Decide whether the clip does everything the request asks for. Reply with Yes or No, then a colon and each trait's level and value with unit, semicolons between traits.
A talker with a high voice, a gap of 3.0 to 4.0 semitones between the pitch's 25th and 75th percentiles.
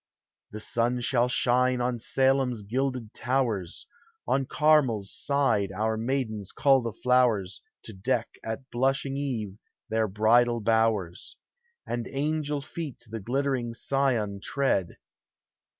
No: low, 120 Hz; average, 3.7 semitones